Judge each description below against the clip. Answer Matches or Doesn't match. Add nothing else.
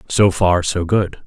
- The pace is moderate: Matches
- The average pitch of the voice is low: Matches